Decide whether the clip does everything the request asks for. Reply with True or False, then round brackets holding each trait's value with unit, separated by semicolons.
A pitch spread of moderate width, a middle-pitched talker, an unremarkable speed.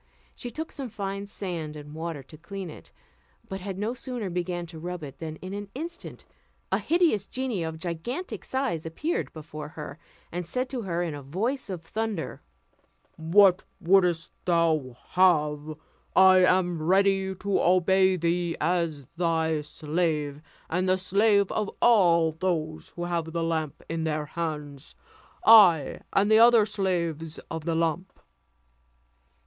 True (3.6 semitones; 175 Hz; 150 wpm)